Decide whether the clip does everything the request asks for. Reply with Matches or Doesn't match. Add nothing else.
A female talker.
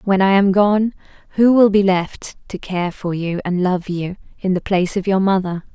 Matches